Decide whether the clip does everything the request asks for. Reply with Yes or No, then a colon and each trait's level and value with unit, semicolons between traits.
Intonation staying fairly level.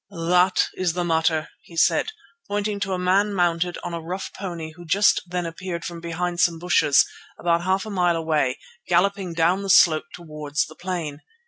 Yes: narrow, 2.1 semitones